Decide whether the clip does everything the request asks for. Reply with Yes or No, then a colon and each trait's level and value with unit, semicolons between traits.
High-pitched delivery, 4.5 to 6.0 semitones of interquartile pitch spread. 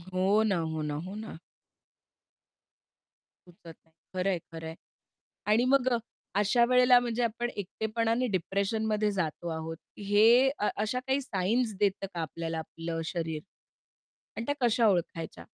Yes: high, 205 Hz; wide, 5.6 semitones